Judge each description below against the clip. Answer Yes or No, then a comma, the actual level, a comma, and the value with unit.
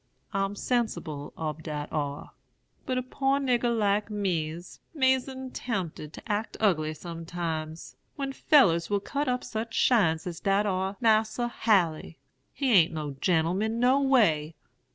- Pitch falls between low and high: No, high, 200 Hz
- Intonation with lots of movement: Yes, wide, 6.9 semitones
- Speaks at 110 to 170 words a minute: Yes, average, 140 wpm